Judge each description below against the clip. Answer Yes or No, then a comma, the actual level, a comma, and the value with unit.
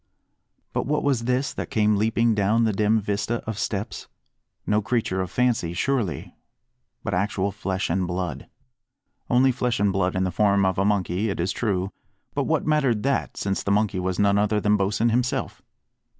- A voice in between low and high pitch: No, low, 105 Hz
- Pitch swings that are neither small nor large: Yes, average, 3.3 semitones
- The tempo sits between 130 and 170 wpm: No, average, 180 wpm